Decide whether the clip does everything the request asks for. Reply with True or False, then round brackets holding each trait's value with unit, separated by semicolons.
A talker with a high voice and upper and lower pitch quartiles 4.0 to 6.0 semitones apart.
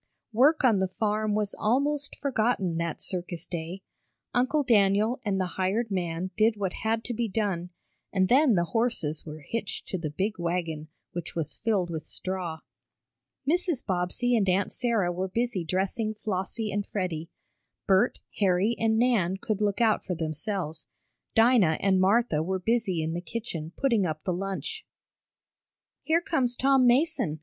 True (200 Hz; 4.7 semitones)